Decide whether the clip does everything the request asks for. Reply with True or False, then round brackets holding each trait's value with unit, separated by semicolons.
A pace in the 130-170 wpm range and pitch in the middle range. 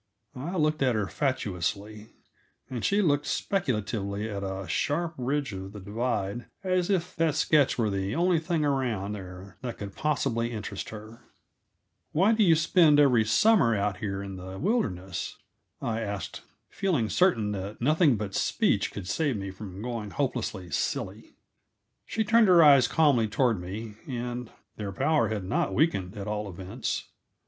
False (160 wpm; 115 Hz)